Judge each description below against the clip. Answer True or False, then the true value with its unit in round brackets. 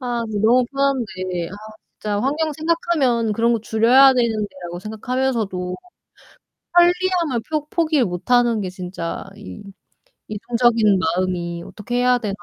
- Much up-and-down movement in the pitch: False (5.0 semitones)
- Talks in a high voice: True (230 Hz)